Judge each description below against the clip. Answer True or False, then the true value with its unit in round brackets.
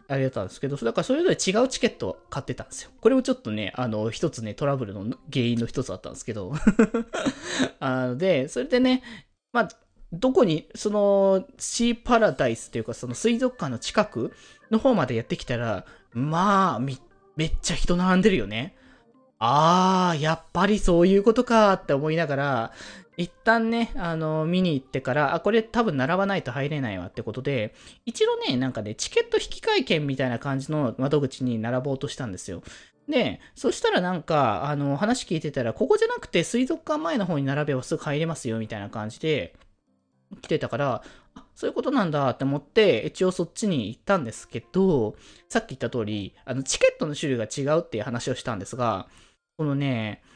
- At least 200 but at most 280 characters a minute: False (385 characters per minute)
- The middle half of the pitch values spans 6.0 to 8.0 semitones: False (8.7 semitones)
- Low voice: False (155 Hz)